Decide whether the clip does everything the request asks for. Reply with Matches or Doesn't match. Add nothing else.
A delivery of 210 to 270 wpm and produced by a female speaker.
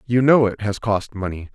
Doesn't match